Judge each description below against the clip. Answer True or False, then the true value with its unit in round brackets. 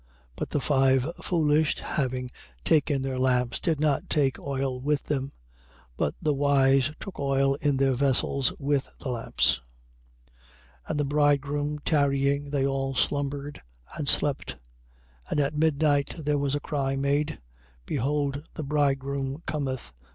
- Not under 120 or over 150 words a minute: True (145 wpm)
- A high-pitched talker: False (140 Hz)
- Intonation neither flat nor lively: False (1.5 semitones)